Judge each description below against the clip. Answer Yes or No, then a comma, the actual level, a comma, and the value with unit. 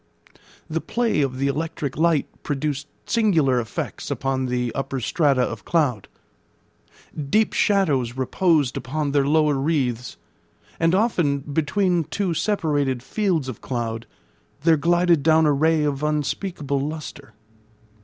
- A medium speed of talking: No, slow, 125 wpm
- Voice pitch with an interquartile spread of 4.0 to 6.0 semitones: No, average, 3.6 semitones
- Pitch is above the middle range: No, medium, 150 Hz